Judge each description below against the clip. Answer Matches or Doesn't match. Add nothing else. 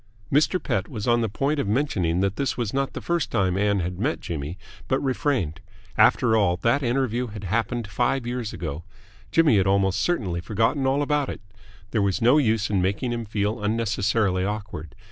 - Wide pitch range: Doesn't match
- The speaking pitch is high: Doesn't match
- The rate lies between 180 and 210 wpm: Matches